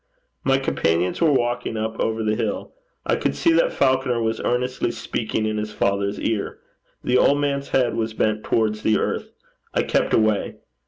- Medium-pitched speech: No, low, 115 Hz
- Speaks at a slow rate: No, average, 175 wpm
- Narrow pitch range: No, average, 3.1 semitones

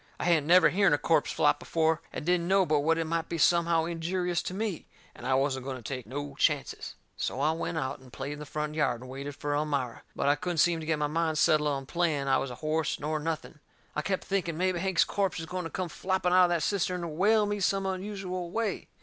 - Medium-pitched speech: Yes, medium, 160 Hz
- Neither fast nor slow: No, fast, 250 wpm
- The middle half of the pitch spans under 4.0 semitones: Yes, average, 3.6 semitones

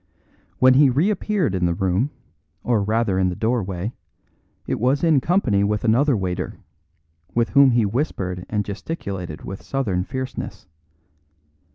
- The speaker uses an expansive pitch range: Yes, wide, 6.0 semitones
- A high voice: No, low, 115 Hz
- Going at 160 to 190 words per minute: No, average, 140 wpm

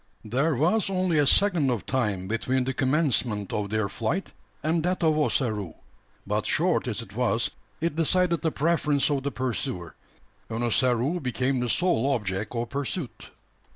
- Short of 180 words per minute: Yes, average, 160 wpm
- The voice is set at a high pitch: No, low, 130 Hz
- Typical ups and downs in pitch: No, wide, 6.0 semitones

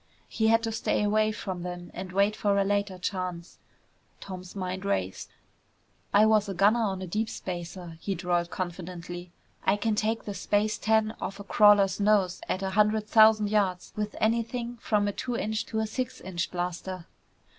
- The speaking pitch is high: Yes, high, 200 Hz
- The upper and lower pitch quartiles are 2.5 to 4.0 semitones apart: Yes, average, 2.9 semitones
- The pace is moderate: Yes, average, 180 wpm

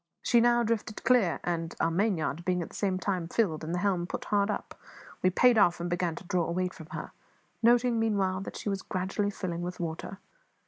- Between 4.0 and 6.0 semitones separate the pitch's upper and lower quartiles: No, average, 3.4 semitones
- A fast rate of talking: Yes, fast, 215 wpm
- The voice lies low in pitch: No, medium, 185 Hz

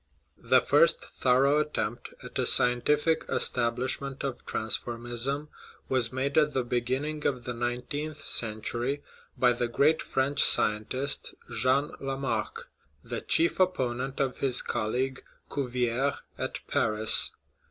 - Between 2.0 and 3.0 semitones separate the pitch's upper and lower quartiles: Yes, average, 2.7 semitones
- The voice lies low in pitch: Yes, low, 130 Hz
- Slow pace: Yes, slow, 120 wpm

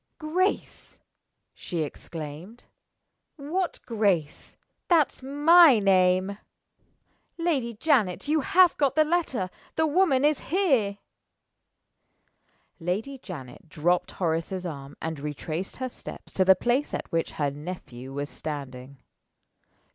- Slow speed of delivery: Yes, slow, 110 wpm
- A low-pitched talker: No, high, 200 Hz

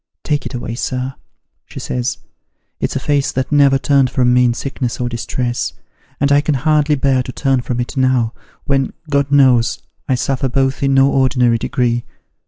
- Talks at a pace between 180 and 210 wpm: Yes, average, 190 wpm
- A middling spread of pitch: No, narrow, 2.1 semitones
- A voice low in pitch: Yes, low, 130 Hz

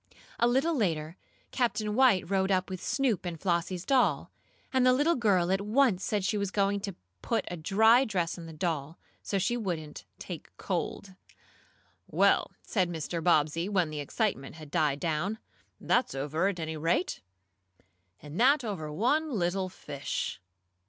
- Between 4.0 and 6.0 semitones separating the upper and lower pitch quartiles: Yes, average, 5.1 semitones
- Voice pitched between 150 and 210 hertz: Yes, medium, 185 Hz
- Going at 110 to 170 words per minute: Yes, average, 160 wpm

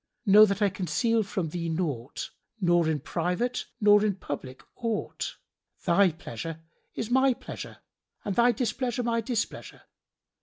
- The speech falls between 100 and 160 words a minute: Yes, average, 140 wpm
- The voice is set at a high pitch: Yes, high, 200 Hz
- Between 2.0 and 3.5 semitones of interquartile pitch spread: No, wide, 5.5 semitones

